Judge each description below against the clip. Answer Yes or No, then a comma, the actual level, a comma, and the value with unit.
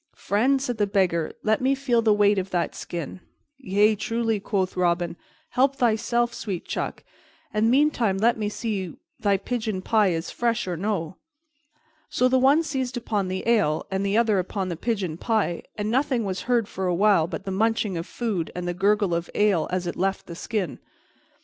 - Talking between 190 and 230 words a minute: Yes, average, 195 wpm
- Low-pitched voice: No, high, 205 Hz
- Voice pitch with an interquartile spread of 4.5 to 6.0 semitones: No, average, 4.1 semitones